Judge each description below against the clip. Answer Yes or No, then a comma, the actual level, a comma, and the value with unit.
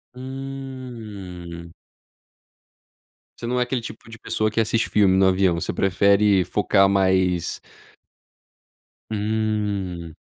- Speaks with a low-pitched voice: Yes, low, 100 Hz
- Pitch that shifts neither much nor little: Yes, average, 3.4 semitones